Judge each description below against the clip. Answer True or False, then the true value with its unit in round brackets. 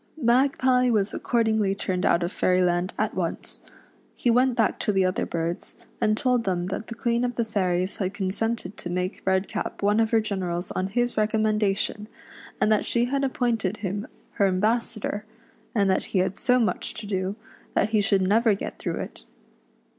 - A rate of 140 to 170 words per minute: False (180 wpm)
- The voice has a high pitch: True (210 Hz)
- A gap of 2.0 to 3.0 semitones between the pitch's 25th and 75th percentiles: False (3.6 semitones)